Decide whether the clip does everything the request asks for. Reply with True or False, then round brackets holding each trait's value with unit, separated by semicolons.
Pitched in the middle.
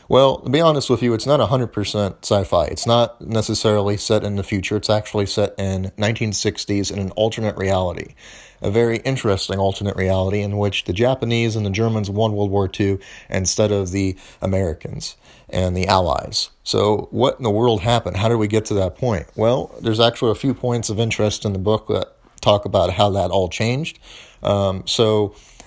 False (105 Hz)